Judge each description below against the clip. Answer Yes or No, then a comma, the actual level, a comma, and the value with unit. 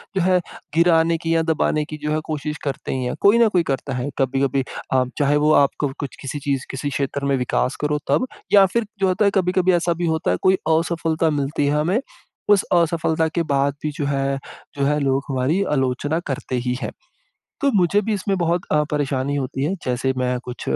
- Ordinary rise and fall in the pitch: Yes, average, 3.9 semitones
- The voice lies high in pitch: No, medium, 150 Hz